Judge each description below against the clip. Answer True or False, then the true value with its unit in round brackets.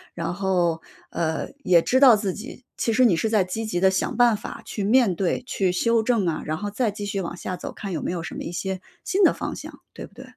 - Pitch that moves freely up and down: False (4.3 semitones)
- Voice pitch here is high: True (195 Hz)